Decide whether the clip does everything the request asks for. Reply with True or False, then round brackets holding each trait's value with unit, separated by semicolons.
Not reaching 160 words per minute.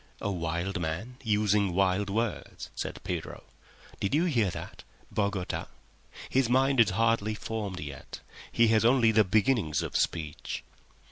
True (135 wpm)